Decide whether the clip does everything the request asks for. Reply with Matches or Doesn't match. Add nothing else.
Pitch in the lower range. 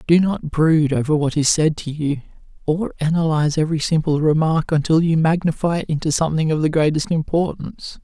Doesn't match